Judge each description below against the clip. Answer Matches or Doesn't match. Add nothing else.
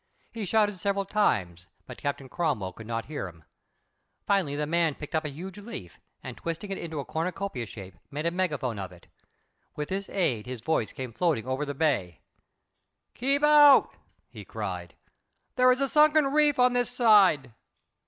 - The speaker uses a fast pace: Doesn't match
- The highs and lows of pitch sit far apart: Matches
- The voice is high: Doesn't match